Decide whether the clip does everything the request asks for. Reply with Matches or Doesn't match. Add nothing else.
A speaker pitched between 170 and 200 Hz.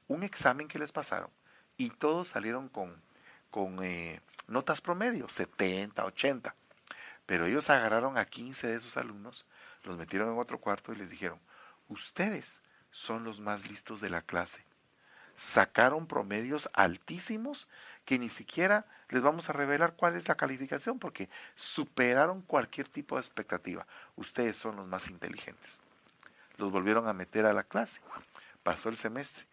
Doesn't match